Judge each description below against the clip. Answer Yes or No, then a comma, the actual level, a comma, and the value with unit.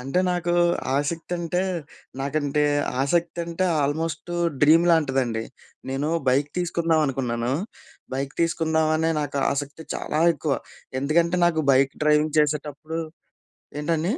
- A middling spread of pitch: Yes, average, 3.0 semitones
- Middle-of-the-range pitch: Yes, medium, 155 Hz